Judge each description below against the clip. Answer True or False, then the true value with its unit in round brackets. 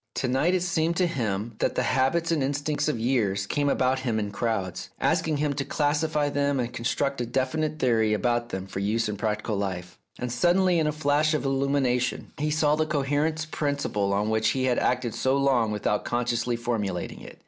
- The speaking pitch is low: True (130 Hz)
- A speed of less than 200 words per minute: False (205 wpm)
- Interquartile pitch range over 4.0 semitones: True (4.8 semitones)